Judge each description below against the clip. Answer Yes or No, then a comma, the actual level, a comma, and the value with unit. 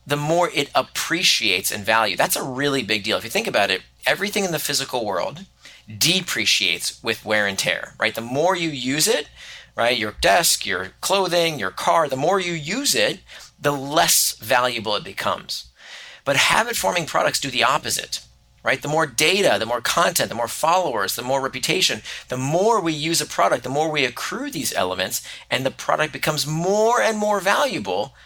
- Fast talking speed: No, average, 185 wpm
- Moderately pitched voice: Yes, medium, 155 Hz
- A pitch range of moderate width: No, wide, 5.9 semitones